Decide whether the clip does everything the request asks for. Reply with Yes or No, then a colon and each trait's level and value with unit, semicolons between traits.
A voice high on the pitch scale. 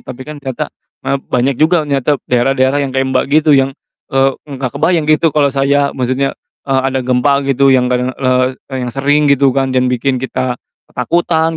No: low, 135 Hz